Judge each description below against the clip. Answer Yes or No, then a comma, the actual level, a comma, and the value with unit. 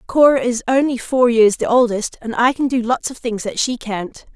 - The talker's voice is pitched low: No, high, 240 Hz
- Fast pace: Yes, fast, 235 wpm